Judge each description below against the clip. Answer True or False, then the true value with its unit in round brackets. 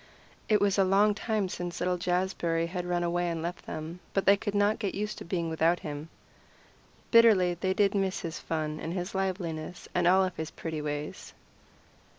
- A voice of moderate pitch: True (180 Hz)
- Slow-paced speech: False (185 wpm)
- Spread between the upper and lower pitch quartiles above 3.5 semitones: False (2.9 semitones)